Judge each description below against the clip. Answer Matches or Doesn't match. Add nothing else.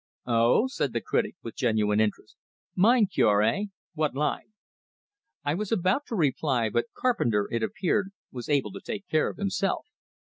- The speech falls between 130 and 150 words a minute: Doesn't match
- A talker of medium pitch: Matches